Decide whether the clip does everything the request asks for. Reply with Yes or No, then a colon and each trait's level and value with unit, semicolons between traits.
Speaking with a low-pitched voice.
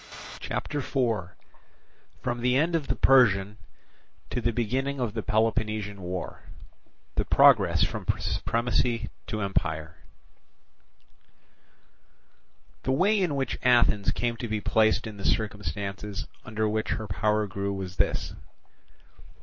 Yes: low, 110 Hz